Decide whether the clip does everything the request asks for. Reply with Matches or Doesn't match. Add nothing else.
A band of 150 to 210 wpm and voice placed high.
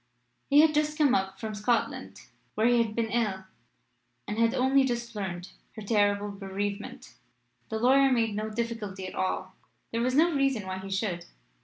Matches